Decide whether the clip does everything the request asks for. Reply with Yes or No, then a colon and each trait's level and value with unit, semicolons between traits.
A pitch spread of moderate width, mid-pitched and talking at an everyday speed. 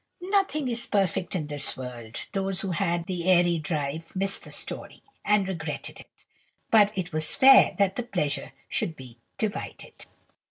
Yes: average, 4.5 semitones; medium, 180 Hz; average, 160 wpm